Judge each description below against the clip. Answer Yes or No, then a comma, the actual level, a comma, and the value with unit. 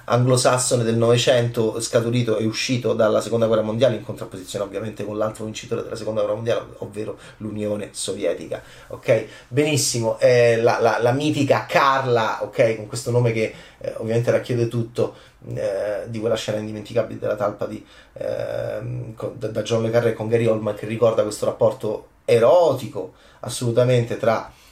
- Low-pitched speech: Yes, low, 115 Hz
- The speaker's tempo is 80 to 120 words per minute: No, average, 155 wpm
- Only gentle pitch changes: Yes, narrow, 2.0 semitones